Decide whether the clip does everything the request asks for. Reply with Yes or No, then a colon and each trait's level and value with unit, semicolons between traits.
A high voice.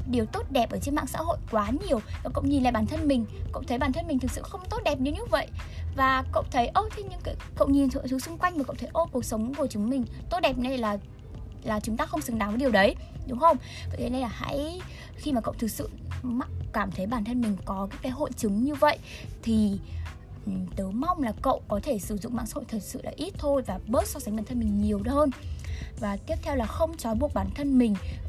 Yes: high, 240 Hz